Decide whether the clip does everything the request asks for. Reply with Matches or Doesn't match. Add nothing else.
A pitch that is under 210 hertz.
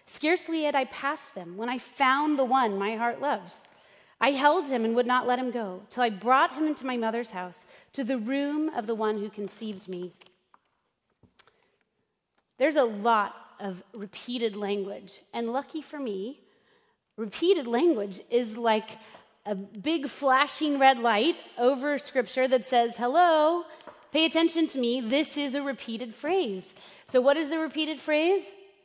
Doesn't match